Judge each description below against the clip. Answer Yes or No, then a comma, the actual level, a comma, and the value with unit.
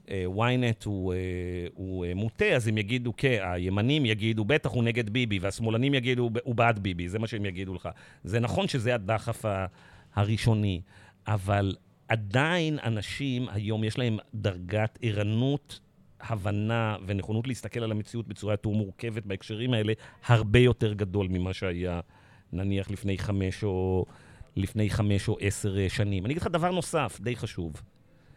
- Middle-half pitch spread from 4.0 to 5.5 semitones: No, average, 3.5 semitones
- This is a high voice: No, low, 110 Hz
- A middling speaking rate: Yes, average, 140 wpm